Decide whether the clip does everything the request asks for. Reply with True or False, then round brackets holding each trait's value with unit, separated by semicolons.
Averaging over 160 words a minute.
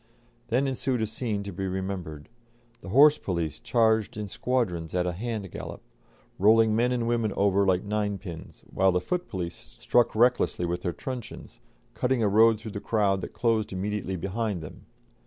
True (175 wpm)